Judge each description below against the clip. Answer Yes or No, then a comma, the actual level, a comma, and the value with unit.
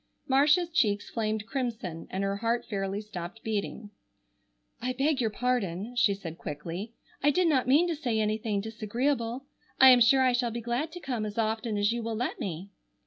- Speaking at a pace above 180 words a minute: Yes, average, 190 wpm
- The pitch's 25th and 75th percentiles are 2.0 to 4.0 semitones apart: Yes, average, 3.7 semitones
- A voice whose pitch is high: Yes, high, 230 Hz